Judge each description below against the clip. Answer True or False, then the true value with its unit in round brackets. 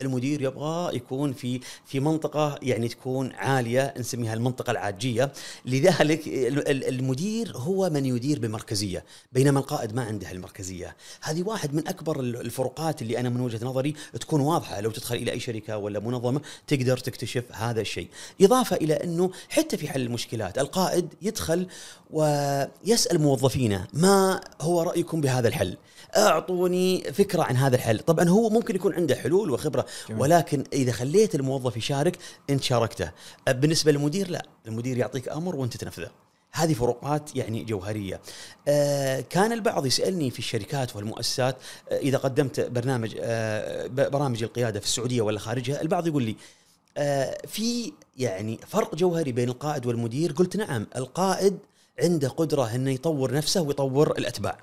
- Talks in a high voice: False (135 Hz)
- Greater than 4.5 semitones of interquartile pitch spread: True (5.0 semitones)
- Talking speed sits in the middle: False (145 wpm)